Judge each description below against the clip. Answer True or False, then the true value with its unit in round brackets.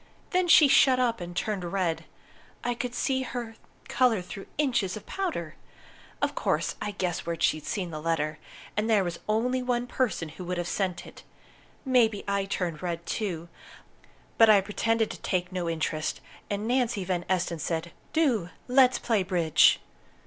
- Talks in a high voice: True (200 Hz)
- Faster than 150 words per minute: True (170 wpm)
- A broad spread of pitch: True (5.7 semitones)